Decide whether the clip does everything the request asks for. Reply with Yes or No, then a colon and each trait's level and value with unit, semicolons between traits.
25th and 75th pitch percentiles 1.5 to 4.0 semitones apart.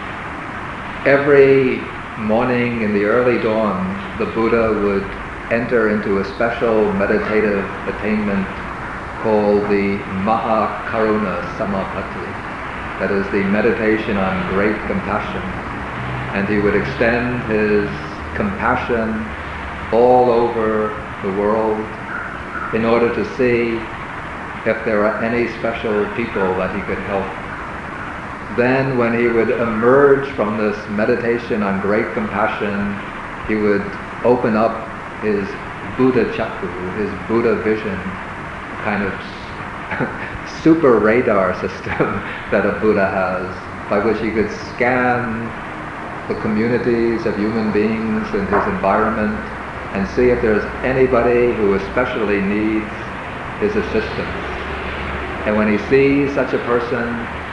Yes: average, 2.8 semitones